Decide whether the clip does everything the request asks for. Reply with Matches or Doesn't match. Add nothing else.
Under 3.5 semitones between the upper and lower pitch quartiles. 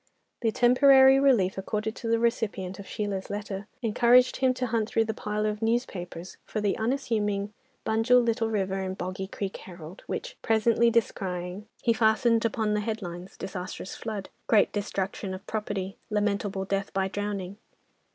Matches